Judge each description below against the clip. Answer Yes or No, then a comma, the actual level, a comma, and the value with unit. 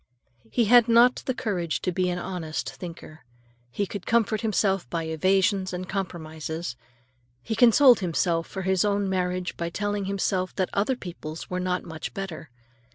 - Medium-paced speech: Yes, average, 160 wpm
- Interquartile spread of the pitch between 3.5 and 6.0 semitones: No, average, 3.1 semitones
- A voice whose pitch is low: No, medium, 185 Hz